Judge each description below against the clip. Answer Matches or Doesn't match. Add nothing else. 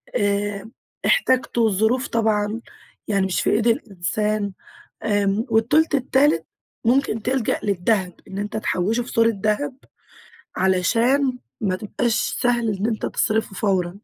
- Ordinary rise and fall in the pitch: Matches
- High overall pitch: Matches